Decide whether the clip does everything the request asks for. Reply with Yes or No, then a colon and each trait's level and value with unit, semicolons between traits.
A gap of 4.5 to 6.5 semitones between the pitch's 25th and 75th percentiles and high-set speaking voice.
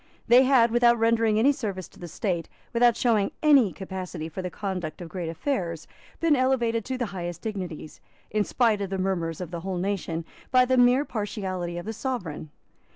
Yes: wide, 5.4 semitones; high, 200 Hz